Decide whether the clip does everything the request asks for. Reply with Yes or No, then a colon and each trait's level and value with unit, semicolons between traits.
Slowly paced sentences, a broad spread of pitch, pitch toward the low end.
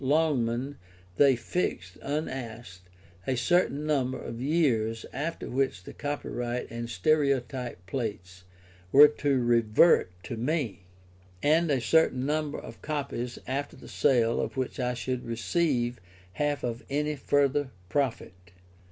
No: slow, 125 wpm; average, 3.8 semitones; low, 130 Hz